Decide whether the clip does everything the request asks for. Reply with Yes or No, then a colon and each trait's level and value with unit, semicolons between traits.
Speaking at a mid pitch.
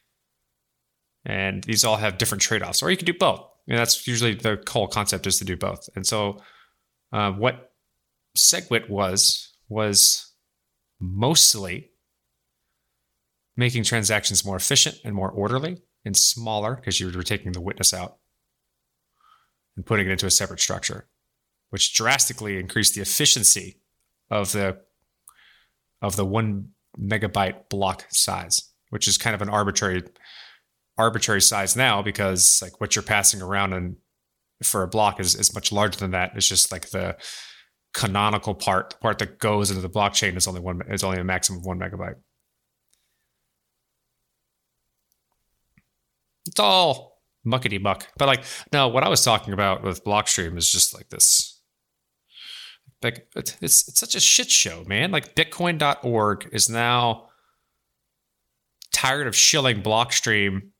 No: low, 100 Hz